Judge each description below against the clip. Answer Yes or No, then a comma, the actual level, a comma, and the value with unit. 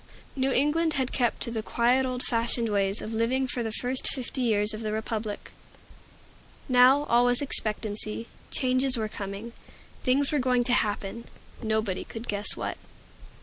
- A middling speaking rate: Yes, average, 160 wpm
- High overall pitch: Yes, high, 235 Hz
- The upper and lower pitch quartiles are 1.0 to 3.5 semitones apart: Yes, average, 3.0 semitones